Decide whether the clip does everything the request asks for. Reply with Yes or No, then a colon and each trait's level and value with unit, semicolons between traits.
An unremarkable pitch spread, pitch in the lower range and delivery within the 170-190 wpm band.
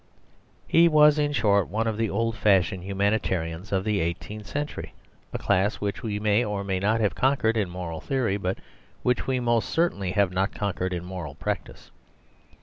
Yes: average, 3.4 semitones; low, 105 Hz; average, 180 wpm